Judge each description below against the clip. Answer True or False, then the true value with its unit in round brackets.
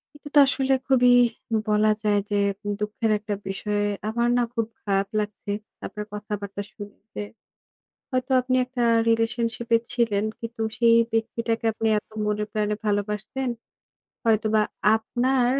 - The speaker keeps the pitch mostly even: True (2.3 semitones)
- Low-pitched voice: False (220 Hz)